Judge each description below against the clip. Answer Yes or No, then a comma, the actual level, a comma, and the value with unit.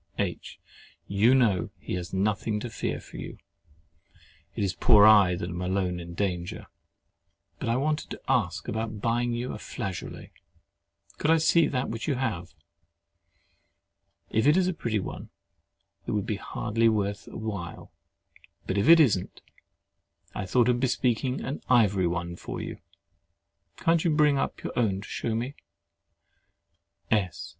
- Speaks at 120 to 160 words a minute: Yes, average, 150 wpm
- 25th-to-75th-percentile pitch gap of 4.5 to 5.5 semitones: Yes, average, 4.9 semitones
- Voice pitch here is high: No, low, 110 Hz